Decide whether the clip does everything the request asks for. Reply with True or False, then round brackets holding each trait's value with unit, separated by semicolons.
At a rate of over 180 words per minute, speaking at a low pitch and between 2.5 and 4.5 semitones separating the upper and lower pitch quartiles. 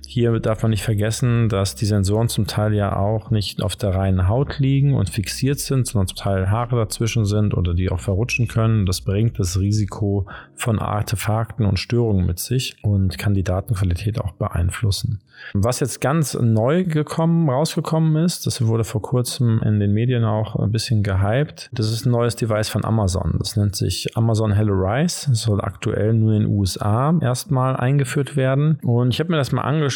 True (190 wpm; 110 Hz; 3.9 semitones)